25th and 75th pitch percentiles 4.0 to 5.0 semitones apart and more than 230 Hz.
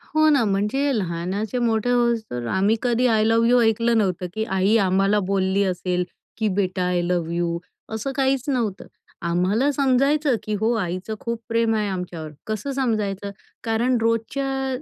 No: average, 4.3 semitones; high, 220 Hz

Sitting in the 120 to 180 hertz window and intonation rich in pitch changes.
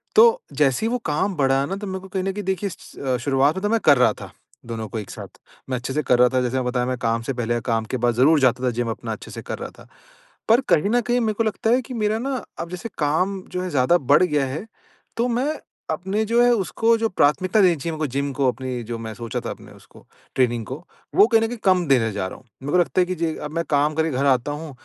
Yes: medium, 150 Hz; wide, 7.6 semitones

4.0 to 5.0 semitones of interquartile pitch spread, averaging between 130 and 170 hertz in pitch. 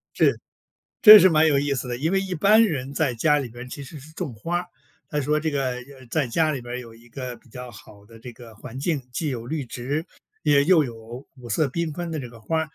Yes: average, 4.6 semitones; medium, 140 Hz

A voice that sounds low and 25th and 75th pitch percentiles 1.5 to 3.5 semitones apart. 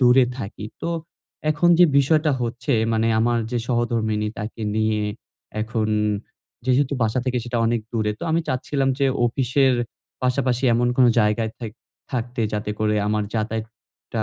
Yes: low, 120 Hz; average, 2.8 semitones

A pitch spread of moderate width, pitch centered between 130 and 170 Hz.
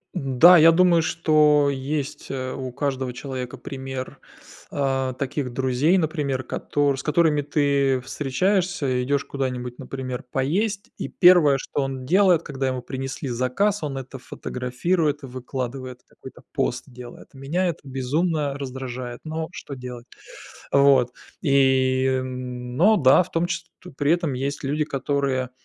Yes: average, 3.0 semitones; low, 135 Hz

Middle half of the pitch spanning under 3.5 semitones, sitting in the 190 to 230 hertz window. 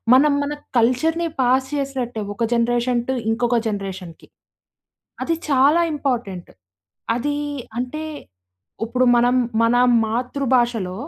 No: average, 2.8 semitones; high, 245 Hz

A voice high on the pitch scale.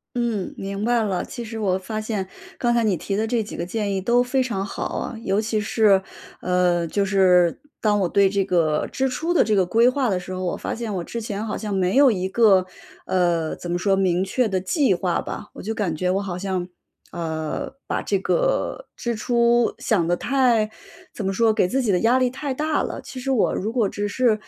Yes: high, 205 Hz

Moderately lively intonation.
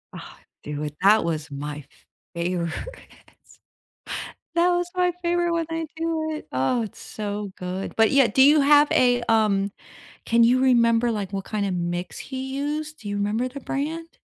No: wide, 7.3 semitones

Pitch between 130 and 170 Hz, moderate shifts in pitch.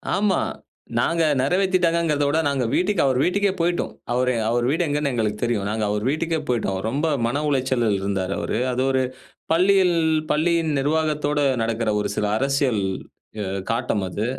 No: medium, 140 Hz; wide, 6.2 semitones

